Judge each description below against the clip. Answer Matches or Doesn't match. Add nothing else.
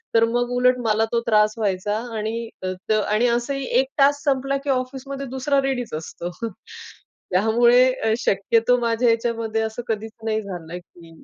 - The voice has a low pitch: Doesn't match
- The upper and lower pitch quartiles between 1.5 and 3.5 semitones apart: Matches